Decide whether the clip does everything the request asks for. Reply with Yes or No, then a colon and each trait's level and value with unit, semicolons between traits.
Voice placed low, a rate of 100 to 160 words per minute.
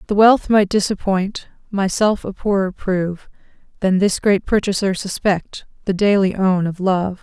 No: high, 195 Hz; average, 150 wpm